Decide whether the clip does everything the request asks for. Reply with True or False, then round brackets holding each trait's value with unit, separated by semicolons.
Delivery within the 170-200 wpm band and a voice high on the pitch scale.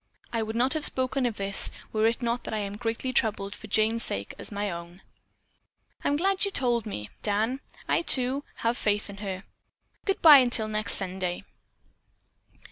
True (185 wpm; 220 Hz)